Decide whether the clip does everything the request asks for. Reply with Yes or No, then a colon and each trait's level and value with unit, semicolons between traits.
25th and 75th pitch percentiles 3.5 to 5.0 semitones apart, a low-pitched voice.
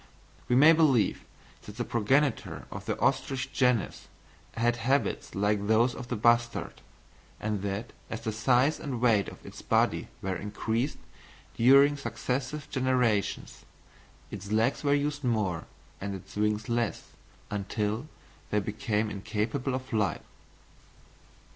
Yes: average, 3.8 semitones; low, 115 Hz